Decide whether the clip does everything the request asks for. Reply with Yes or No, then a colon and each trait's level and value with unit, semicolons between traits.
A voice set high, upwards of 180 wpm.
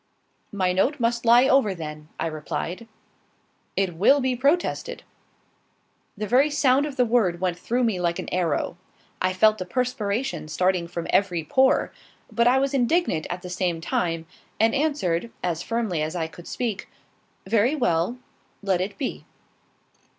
No: high, 200 Hz; average, 160 wpm